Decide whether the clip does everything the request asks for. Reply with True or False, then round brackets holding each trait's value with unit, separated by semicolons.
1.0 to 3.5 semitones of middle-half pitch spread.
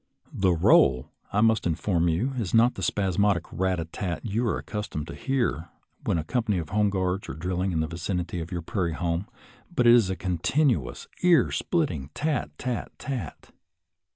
False (5.1 semitones)